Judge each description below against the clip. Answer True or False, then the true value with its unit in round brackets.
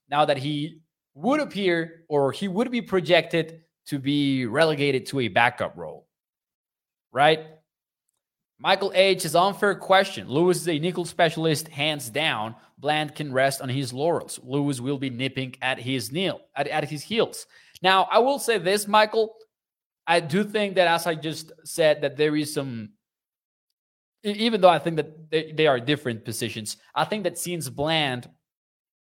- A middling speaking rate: True (165 wpm)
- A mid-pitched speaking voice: True (155 Hz)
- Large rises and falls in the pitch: False (4.5 semitones)